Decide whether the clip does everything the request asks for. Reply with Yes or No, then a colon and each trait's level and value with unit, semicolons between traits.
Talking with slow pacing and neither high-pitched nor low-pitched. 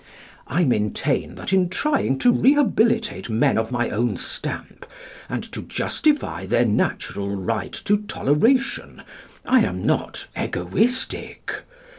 Yes: slow, 120 wpm; medium, 175 Hz